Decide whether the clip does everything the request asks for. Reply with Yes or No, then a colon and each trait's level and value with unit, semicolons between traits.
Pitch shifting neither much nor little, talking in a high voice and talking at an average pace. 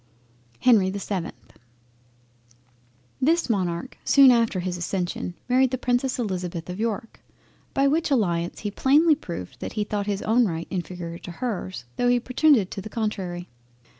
No: wide, 5.7 semitones; high, 210 Hz; average, 155 wpm